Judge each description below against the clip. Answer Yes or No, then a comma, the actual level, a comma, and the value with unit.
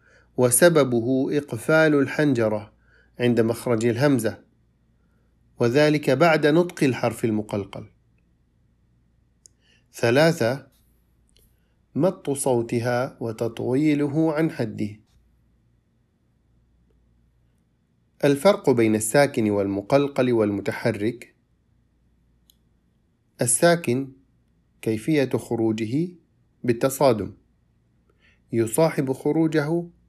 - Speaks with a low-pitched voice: Yes, low, 120 Hz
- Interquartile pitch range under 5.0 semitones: No, average, 5.3 semitones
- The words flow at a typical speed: No, slow, 55 wpm